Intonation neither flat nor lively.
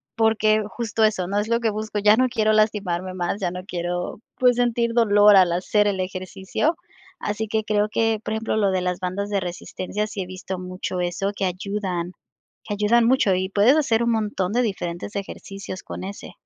Yes: average, 3.0 semitones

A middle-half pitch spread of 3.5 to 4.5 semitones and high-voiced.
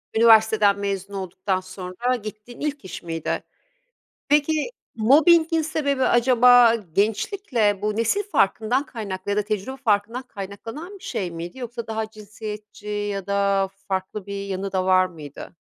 Yes: average, 3.9 semitones; high, 210 Hz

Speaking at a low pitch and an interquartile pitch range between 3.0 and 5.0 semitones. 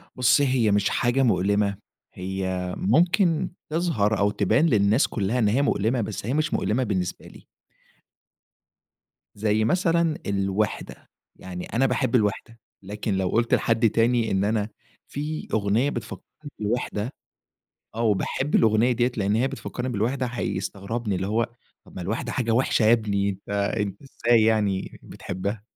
Yes: low, 110 Hz; average, 3.6 semitones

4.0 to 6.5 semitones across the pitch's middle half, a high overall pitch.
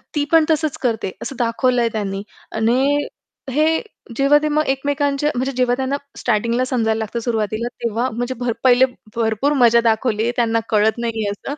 No: average, 3.5 semitones; high, 240 Hz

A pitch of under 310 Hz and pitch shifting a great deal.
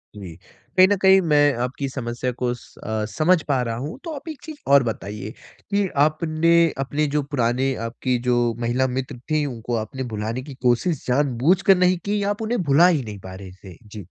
Yes: low, 135 Hz; wide, 6.1 semitones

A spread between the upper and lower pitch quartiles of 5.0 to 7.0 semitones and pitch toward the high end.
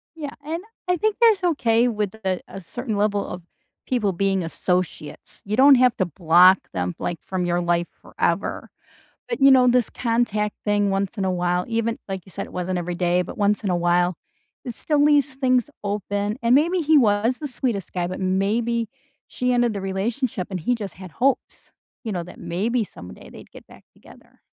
Yes: wide, 5.4 semitones; high, 205 Hz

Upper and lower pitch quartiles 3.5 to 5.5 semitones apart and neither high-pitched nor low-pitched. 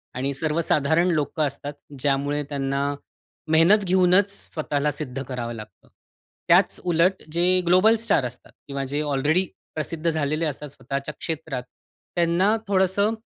Yes: average, 4.2 semitones; medium, 155 Hz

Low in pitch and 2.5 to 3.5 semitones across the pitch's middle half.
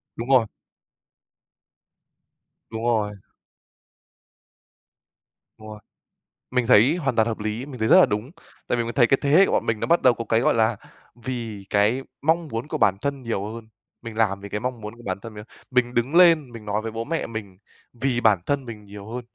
Yes: low, 115 Hz; average, 3.1 semitones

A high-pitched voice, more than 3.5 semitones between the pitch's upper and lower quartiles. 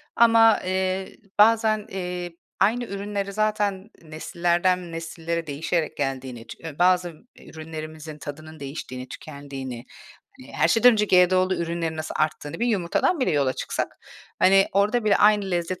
No: medium, 180 Hz; average, 4.4 semitones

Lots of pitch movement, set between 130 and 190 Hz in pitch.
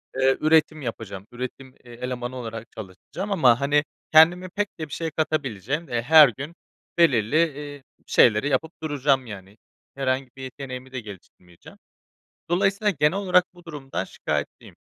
No: average, 4.6 semitones; low, 135 Hz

